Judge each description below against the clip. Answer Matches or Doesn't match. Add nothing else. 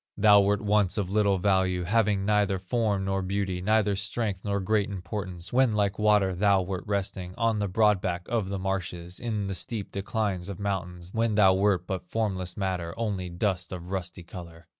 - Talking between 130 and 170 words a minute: Doesn't match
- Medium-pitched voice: Doesn't match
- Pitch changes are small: Matches